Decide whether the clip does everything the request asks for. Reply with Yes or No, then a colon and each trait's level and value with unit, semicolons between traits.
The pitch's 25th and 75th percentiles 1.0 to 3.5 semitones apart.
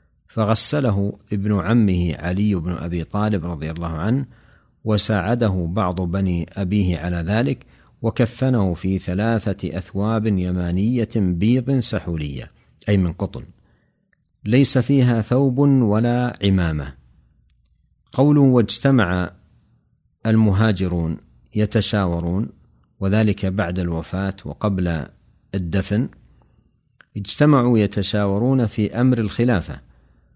No: average, 4.4 semitones